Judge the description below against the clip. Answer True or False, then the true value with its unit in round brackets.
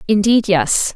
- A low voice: False (210 Hz)